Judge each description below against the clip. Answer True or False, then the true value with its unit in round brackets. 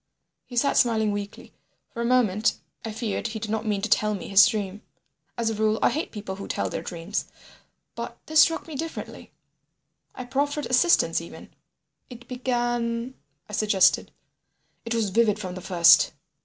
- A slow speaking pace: False (170 wpm)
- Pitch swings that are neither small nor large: True (3.0 semitones)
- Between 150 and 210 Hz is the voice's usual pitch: False (220 Hz)